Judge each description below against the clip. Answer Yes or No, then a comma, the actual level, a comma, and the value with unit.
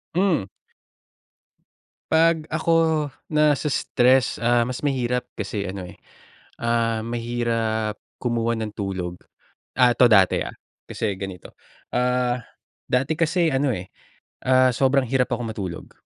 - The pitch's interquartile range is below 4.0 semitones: Yes, average, 3.6 semitones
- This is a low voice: Yes, low, 120 Hz